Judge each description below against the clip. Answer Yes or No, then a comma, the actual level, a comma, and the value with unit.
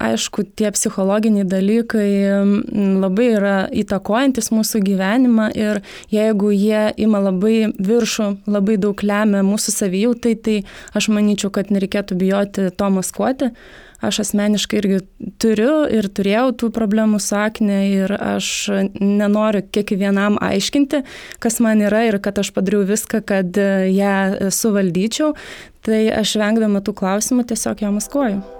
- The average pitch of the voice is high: Yes, high, 210 Hz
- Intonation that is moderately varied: No, narrow, 1.8 semitones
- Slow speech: Yes, slow, 130 wpm